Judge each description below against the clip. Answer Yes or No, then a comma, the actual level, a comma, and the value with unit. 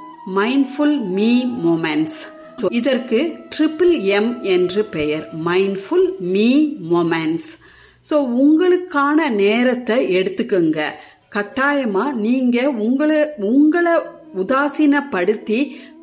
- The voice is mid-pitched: No, very high, 250 Hz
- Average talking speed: No, slow, 65 wpm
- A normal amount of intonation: No, wide, 7.4 semitones